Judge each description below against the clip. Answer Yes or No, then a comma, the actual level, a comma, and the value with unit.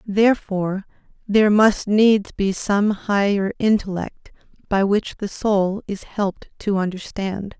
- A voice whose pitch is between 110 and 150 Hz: No, high, 200 Hz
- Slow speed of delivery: Yes, slow, 125 wpm